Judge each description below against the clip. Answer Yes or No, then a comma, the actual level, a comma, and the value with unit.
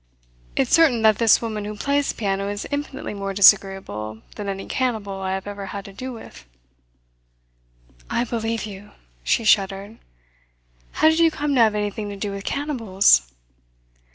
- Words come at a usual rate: Yes, average, 165 wpm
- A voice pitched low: No, high, 205 Hz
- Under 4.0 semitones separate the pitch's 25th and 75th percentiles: Yes, average, 3.0 semitones